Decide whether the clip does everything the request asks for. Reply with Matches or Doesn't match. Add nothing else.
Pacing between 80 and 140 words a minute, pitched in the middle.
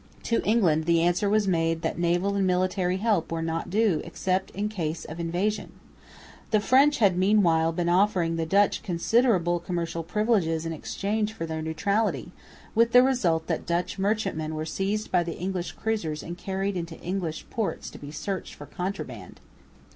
Doesn't match